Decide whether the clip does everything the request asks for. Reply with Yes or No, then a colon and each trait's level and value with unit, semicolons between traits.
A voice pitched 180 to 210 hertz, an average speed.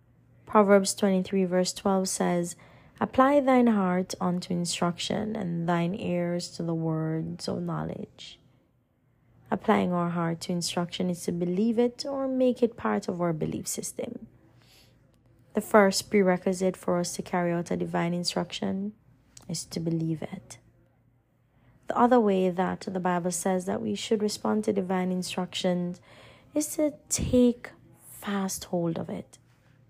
Yes: medium, 185 Hz; average, 145 wpm